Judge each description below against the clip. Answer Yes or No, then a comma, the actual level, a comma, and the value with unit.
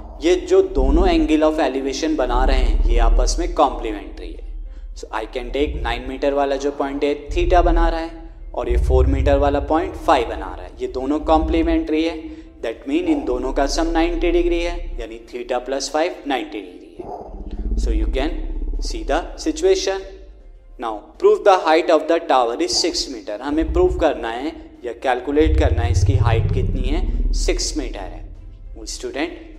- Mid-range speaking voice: Yes, medium, 160 Hz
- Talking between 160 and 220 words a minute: Yes, average, 180 wpm